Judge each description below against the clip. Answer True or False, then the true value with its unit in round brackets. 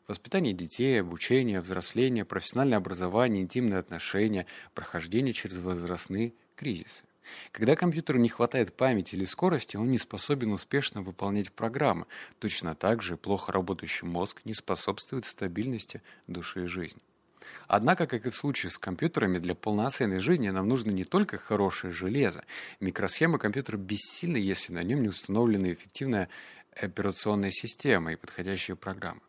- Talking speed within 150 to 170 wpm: False (135 wpm)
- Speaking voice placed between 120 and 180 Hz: False (100 Hz)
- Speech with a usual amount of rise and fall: True (4.4 semitones)